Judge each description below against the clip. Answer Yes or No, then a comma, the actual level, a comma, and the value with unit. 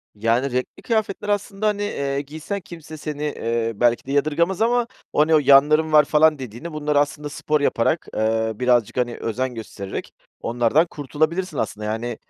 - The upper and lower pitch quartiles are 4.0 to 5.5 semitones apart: Yes, average, 4.7 semitones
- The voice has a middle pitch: Yes, medium, 145 Hz